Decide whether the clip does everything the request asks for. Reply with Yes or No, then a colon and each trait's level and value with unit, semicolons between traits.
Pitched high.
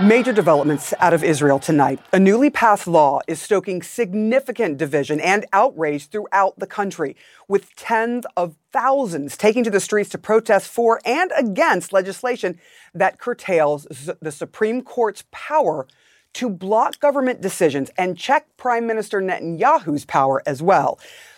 Yes: high, 200 Hz